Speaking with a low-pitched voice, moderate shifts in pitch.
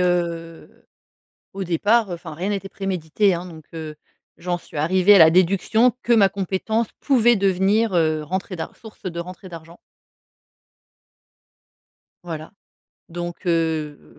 No: medium, 180 Hz; average, 3.0 semitones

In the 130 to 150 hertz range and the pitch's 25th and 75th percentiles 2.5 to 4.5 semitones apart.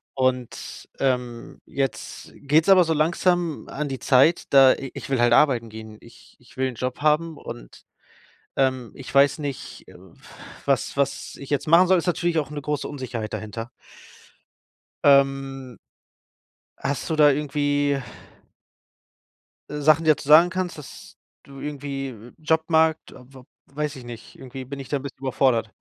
Yes: medium, 140 Hz; average, 2.9 semitones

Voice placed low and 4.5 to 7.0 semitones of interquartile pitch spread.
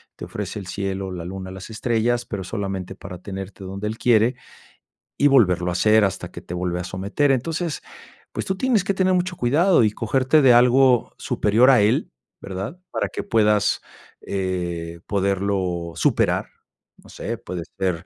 Yes: low, 100 Hz; average, 5.0 semitones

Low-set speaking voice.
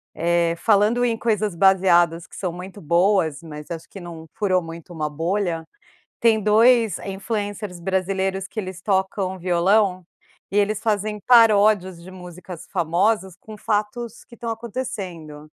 No: high, 190 Hz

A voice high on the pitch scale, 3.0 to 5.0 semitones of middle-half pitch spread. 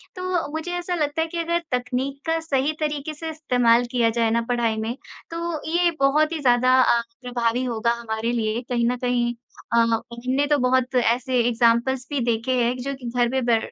Yes: very high, 255 Hz; average, 4.1 semitones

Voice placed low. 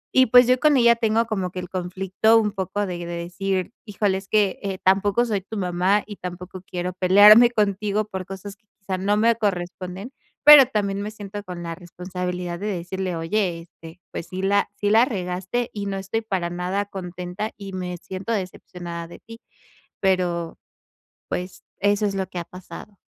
No: high, 195 Hz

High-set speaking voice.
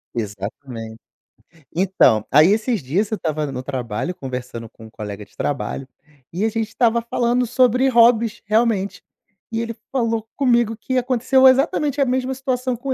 Yes: high, 225 Hz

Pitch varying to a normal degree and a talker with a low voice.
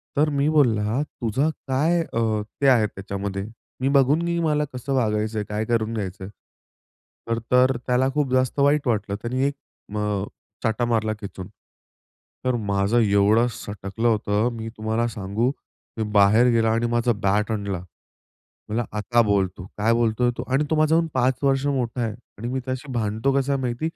Yes: average, 3.9 semitones; low, 115 Hz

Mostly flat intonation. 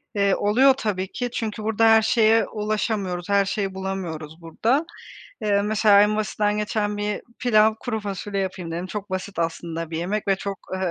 Yes: narrow, 2.3 semitones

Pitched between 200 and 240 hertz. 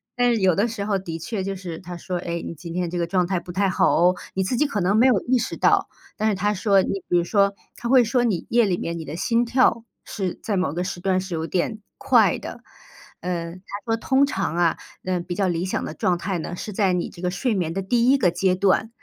No: high, 190 Hz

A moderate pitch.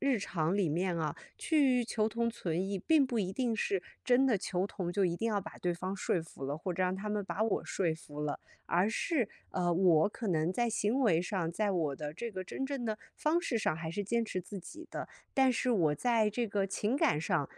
No: high, 200 Hz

